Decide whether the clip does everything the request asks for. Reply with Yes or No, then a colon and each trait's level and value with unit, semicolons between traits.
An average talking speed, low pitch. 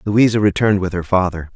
Yes: average, 195 wpm; low, 100 Hz